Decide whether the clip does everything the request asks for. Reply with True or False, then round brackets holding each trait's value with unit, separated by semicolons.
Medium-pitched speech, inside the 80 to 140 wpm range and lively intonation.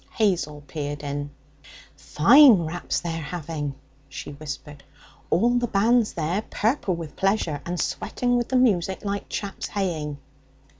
True (175 Hz; 135 wpm; 6.1 semitones)